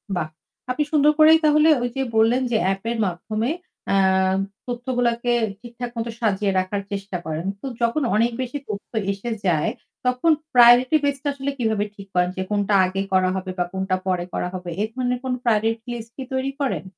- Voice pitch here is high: Yes, high, 225 Hz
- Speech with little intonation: No, average, 4.6 semitones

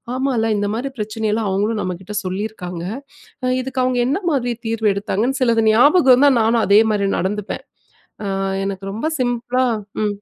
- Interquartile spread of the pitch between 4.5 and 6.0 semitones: No, average, 3.7 semitones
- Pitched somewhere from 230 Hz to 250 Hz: No, high, 220 Hz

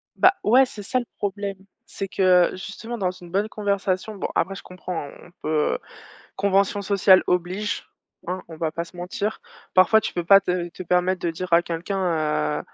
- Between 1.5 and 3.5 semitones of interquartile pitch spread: Yes, narrow, 2.4 semitones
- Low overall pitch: No, medium, 185 Hz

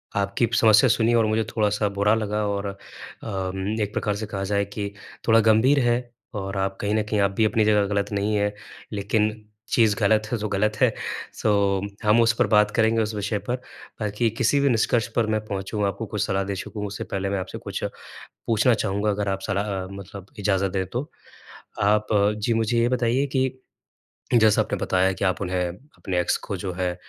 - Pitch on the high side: No, low, 105 Hz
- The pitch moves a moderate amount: No, narrow, 2.0 semitones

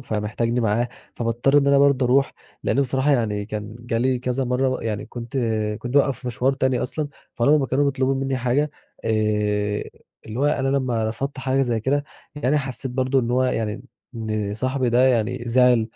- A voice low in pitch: Yes, low, 125 Hz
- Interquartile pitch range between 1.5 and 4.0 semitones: Yes, average, 2.9 semitones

